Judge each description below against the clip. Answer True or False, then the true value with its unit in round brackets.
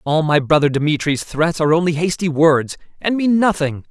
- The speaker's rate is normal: True (185 wpm)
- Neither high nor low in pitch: True (160 Hz)